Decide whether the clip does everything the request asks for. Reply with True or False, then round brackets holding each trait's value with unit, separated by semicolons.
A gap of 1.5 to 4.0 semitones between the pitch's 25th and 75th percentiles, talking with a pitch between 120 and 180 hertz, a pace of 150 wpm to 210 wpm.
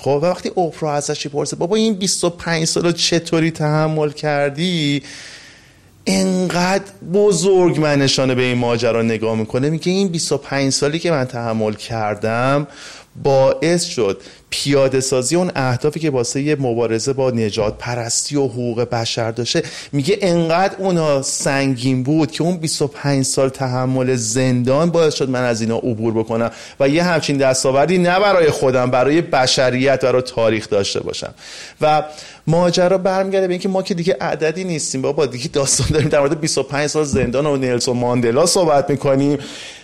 False (4.6 semitones; 140 Hz; 155 wpm)